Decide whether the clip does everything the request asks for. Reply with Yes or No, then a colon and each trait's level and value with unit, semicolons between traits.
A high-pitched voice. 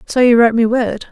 Yes: high, 235 Hz